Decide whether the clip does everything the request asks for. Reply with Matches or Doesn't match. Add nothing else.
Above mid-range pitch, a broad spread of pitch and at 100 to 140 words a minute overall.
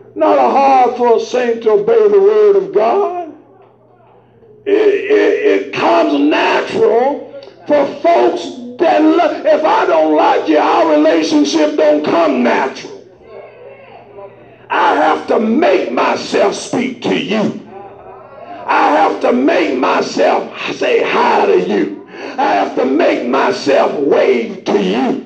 Matches